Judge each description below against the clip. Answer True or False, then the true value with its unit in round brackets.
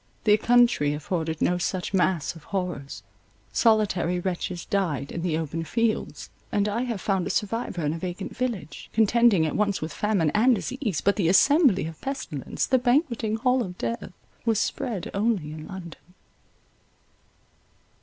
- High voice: True (195 Hz)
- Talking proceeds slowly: False (155 wpm)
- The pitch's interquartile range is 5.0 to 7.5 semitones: True (5.5 semitones)